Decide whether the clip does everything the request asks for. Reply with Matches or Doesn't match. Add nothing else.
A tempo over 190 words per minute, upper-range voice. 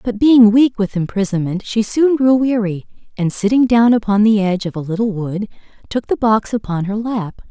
Matches